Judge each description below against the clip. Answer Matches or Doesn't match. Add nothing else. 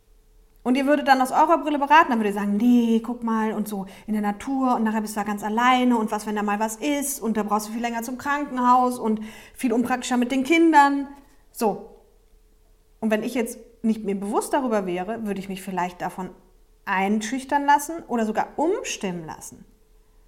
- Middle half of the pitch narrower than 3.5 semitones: Doesn't match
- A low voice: Doesn't match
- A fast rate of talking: Matches